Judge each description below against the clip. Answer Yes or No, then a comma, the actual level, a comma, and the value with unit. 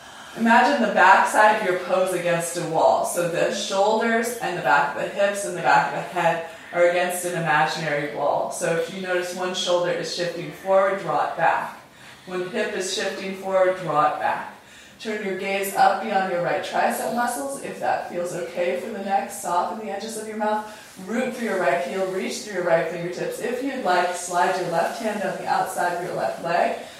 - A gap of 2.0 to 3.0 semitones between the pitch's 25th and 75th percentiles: Yes, narrow, 2.5 semitones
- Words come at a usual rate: No, fast, 215 wpm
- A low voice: No, medium, 185 Hz